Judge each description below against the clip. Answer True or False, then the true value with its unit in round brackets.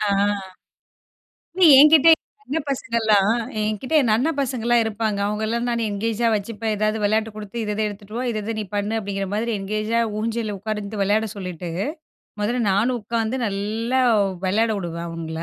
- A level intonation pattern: True (2.2 semitones)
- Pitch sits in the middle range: False (215 Hz)